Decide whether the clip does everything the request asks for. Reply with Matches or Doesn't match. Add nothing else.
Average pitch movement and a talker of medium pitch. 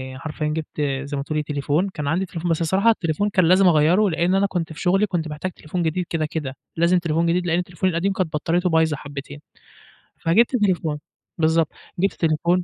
Matches